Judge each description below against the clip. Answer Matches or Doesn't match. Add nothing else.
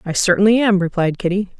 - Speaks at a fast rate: Doesn't match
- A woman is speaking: Matches